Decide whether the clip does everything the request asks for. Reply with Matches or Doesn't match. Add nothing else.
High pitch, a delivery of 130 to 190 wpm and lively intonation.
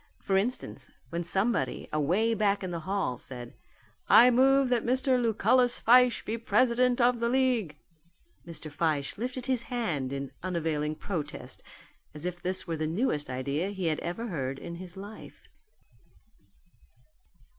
Matches